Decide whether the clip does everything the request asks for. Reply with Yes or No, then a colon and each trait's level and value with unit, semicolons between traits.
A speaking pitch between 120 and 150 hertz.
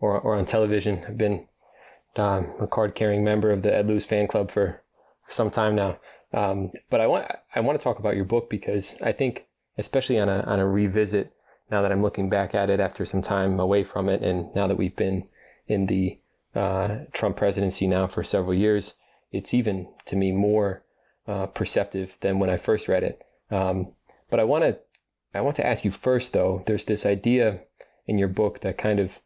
No: low, 100 Hz